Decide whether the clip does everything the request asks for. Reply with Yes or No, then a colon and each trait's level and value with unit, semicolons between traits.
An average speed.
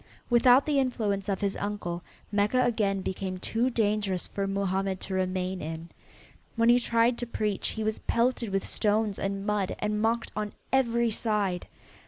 Yes: average, 165 wpm